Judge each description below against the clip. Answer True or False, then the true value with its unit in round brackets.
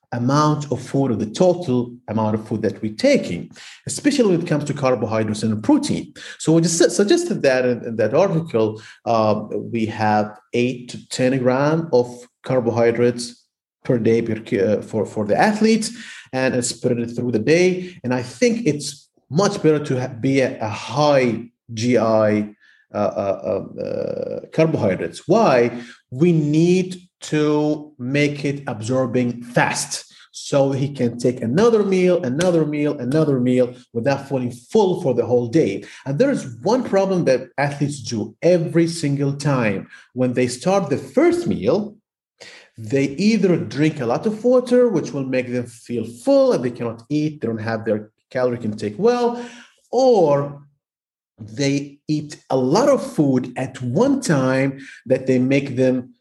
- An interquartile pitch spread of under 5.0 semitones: False (5.6 semitones)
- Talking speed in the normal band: True (155 wpm)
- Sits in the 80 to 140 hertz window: True (135 Hz)